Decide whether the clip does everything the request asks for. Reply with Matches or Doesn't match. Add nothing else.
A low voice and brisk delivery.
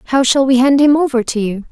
Doesn't match